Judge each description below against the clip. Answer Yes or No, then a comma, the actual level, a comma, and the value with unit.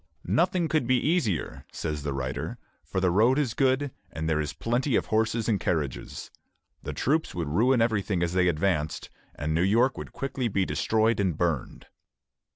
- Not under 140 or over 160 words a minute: No, average, 175 wpm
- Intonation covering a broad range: Yes, wide, 7.5 semitones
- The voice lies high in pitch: No, low, 105 Hz